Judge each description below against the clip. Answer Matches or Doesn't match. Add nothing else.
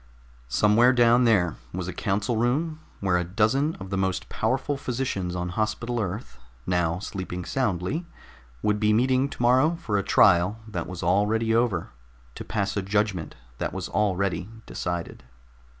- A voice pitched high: Doesn't match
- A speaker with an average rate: Matches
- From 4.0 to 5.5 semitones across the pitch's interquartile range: Matches